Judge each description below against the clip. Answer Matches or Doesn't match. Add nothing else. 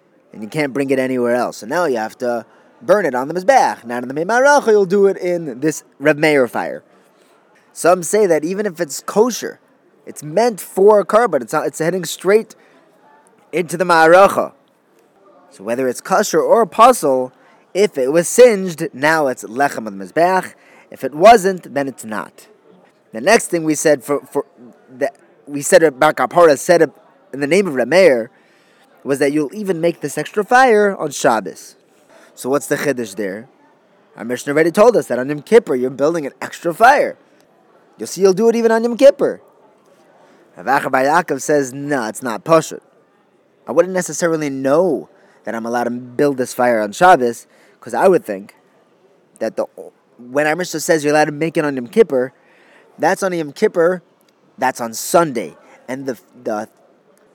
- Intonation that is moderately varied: Doesn't match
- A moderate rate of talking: Matches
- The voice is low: Doesn't match